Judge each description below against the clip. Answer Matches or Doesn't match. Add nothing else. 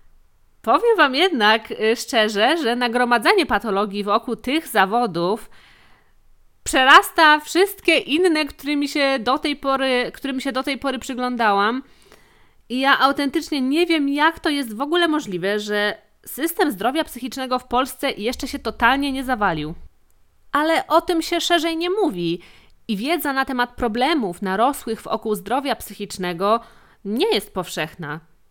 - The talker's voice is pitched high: Matches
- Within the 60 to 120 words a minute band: Doesn't match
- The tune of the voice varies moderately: Doesn't match